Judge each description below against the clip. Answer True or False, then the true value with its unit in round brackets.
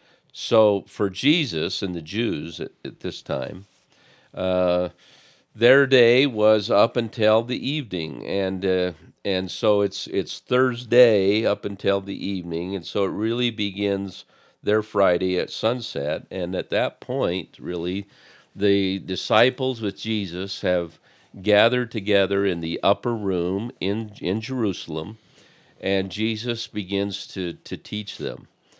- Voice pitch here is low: True (100 Hz)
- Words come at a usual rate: False (130 wpm)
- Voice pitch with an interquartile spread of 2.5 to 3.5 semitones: True (3.1 semitones)